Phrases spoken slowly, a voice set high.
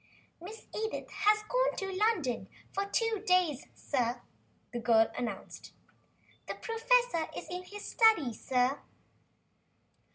Yes: slow, 120 wpm; very high, 370 Hz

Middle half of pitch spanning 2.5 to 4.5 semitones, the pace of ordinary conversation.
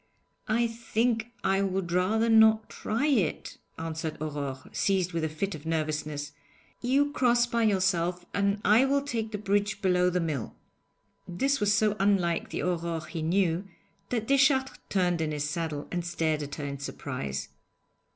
No: wide, 5.4 semitones; average, 160 wpm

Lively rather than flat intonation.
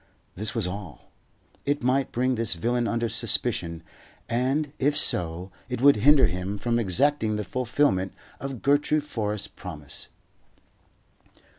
Yes: wide, 5.9 semitones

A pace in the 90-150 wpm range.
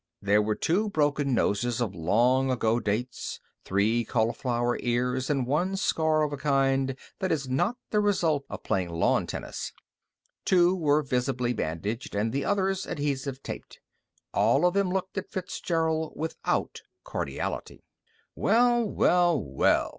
Yes: average, 140 wpm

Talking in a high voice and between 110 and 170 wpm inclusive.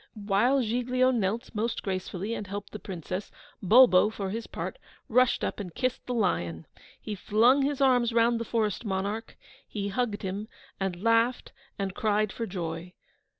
Yes: high, 215 Hz; average, 160 wpm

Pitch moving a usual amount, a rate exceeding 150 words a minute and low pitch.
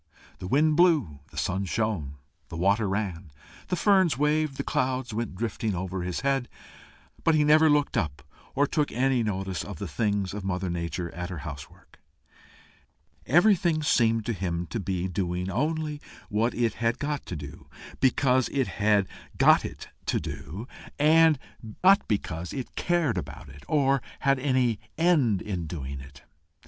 No: wide, 7.9 semitones; average, 165 wpm; low, 110 Hz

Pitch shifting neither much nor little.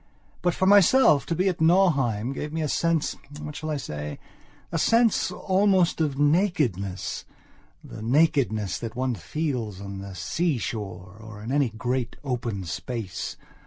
No: wide, 7.2 semitones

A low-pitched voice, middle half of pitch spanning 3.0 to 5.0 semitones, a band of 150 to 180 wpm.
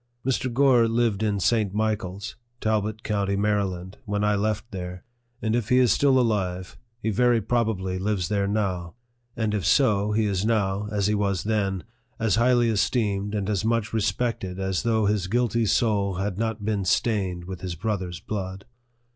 No: low, 105 Hz; narrow, 2.6 semitones; average, 175 wpm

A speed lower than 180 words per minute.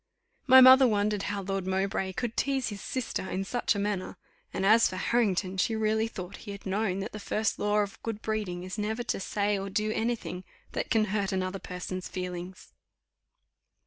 No: average, 195 wpm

